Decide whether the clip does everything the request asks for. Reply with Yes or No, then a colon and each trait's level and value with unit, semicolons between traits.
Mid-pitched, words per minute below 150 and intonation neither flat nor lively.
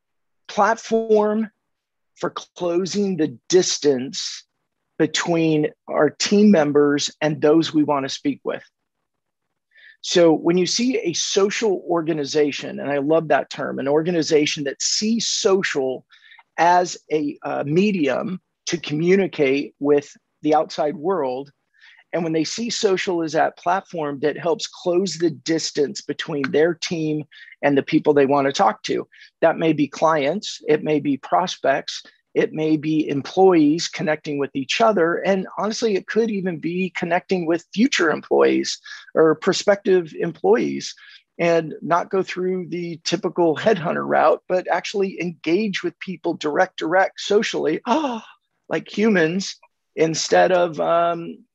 Yes: medium, 170 Hz; slow, 135 wpm; average, 4.1 semitones